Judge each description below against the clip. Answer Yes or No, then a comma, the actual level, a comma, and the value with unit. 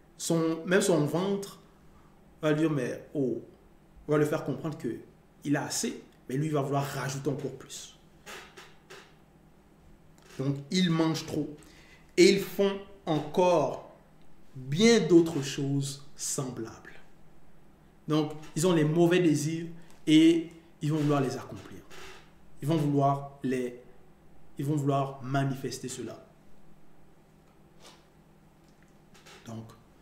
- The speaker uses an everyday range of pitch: Yes, average, 3.7 semitones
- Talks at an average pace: No, slow, 120 wpm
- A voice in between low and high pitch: Yes, medium, 165 Hz